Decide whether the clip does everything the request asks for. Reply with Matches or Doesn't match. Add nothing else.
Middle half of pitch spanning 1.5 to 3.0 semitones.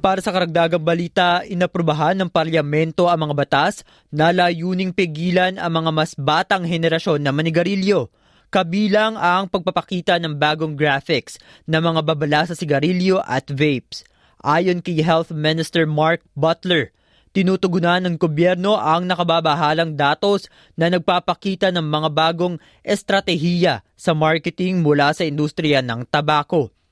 Matches